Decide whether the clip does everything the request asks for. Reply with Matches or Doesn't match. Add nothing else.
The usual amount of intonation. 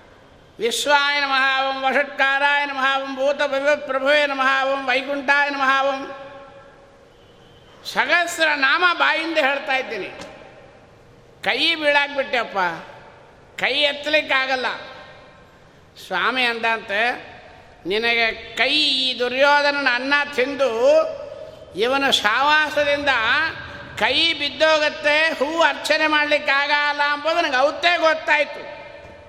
Doesn't match